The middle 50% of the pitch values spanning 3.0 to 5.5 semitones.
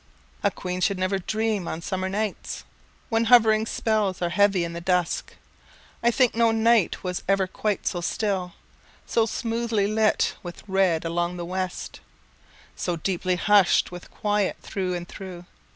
Yes: average, 3.3 semitones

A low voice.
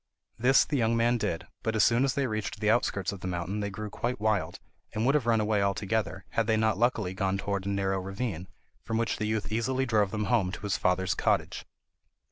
Yes: low, 110 Hz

